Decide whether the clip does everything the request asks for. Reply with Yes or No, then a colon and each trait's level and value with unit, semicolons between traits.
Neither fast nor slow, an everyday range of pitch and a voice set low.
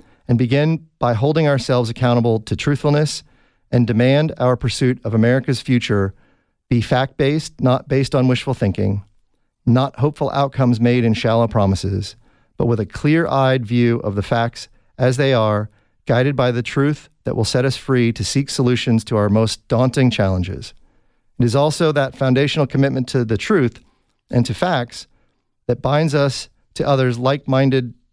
Yes: average, 165 wpm; average, 3.2 semitones; low, 125 Hz